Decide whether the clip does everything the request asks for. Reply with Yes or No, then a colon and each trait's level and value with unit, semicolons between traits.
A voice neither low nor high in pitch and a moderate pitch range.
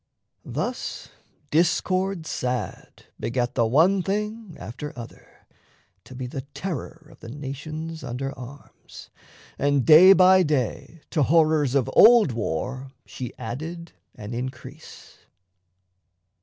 Yes: medium, 145 Hz; average, 4.7 semitones